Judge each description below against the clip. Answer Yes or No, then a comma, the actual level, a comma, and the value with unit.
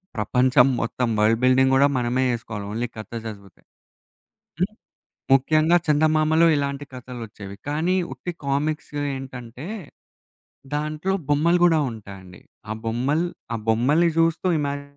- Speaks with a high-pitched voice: No, low, 135 Hz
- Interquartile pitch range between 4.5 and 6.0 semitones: Yes, average, 4.9 semitones